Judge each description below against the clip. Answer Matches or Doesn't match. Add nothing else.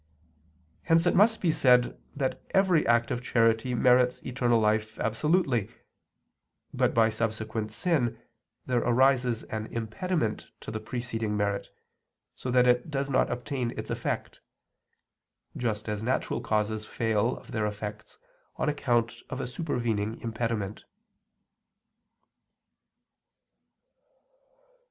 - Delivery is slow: Matches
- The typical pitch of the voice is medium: Doesn't match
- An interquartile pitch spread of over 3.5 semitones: Doesn't match